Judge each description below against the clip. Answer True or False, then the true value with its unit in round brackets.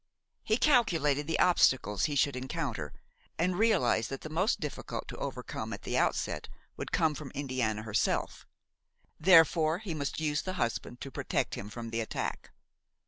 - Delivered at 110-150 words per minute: False (160 wpm)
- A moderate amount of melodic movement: False (5.7 semitones)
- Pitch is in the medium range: True (145 Hz)